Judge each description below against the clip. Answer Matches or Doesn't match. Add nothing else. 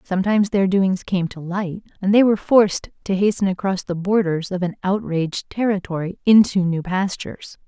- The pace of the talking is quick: Doesn't match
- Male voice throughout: Doesn't match